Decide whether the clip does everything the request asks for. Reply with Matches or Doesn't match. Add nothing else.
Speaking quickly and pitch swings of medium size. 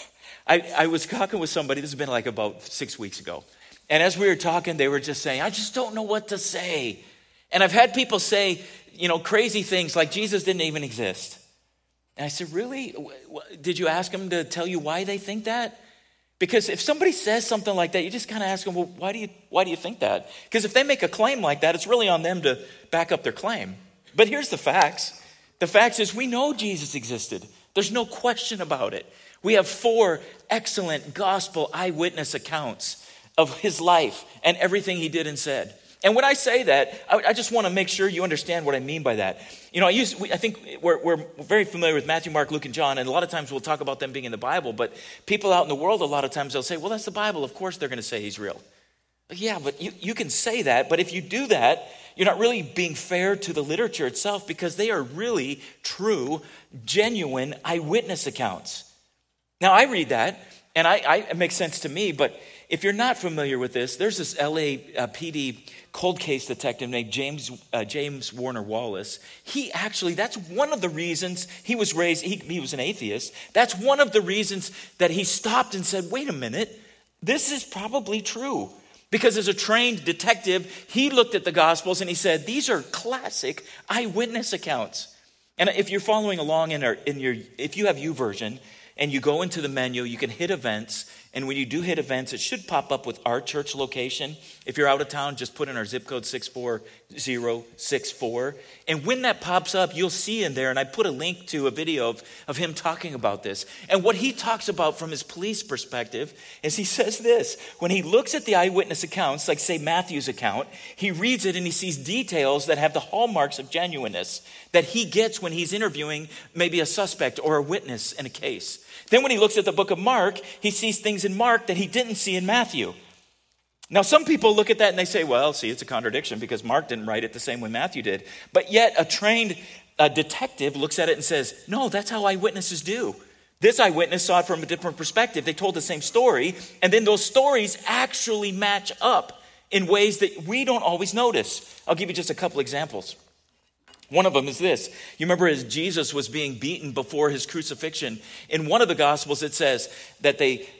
Doesn't match